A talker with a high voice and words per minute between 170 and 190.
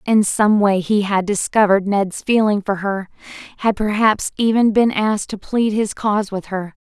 Yes: high, 205 Hz; average, 185 wpm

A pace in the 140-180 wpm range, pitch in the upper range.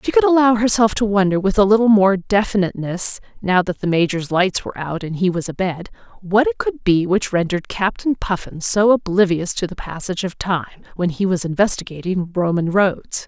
No: average, 195 wpm; high, 195 Hz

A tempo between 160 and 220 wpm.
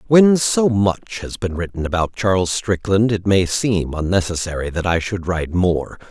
Yes: average, 175 wpm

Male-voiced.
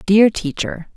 No: female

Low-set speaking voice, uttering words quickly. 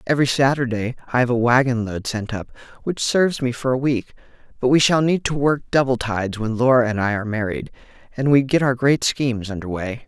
Yes: low, 125 Hz; fast, 220 wpm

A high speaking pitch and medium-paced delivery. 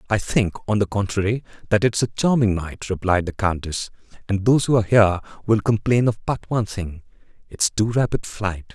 No: low, 105 Hz; average, 190 wpm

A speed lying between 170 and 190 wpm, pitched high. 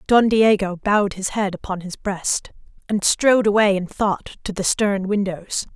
Yes: average, 175 wpm; high, 200 Hz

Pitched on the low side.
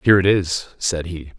Yes: very low, 90 Hz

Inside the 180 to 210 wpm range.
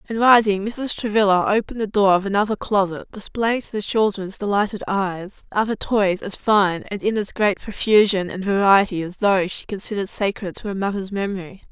Yes: average, 185 wpm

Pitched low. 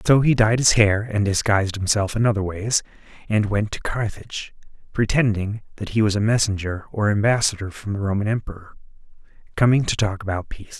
Yes: low, 105 Hz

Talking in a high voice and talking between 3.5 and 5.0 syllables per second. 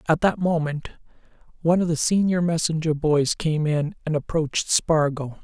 No: medium, 160 Hz; 4.9 syllables/s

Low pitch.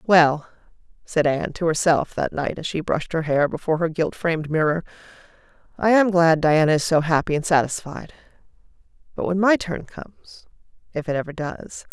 No: medium, 165 Hz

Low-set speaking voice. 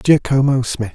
Yes: low, 125 Hz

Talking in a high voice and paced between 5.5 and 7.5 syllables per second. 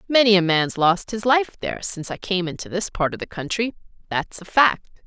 Yes: high, 200 Hz; 5.7 syllables/s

